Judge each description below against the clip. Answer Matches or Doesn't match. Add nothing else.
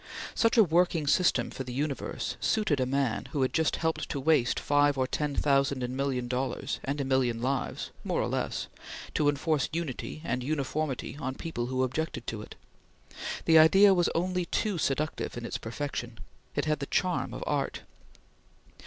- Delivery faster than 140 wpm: Matches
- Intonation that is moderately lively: Matches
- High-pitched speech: Doesn't match